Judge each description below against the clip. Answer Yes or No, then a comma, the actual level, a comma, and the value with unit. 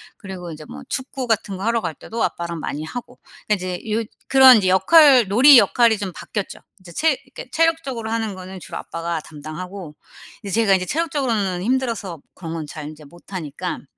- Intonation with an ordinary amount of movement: No, wide, 5.7 semitones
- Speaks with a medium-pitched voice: No, high, 195 Hz